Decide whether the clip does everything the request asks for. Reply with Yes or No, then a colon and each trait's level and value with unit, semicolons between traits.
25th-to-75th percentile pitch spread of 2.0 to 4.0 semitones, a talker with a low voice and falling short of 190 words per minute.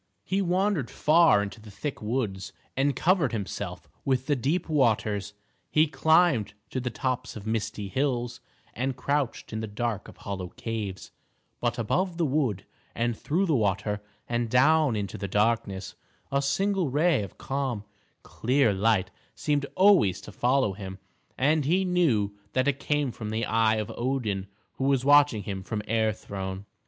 No: wide, 5.5 semitones; low, 120 Hz; average, 165 wpm